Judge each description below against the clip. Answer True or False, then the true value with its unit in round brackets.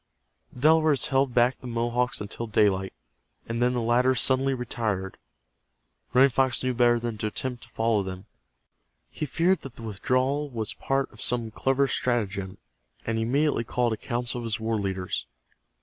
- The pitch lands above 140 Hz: False (120 Hz)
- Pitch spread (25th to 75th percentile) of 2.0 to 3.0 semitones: True (2.7 semitones)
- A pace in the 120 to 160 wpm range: False (170 wpm)